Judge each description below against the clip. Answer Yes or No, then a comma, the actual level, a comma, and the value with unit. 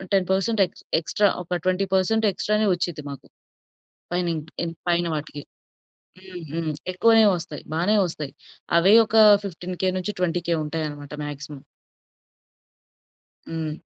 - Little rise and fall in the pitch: No, average, 3.3 semitones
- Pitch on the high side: No, medium, 175 Hz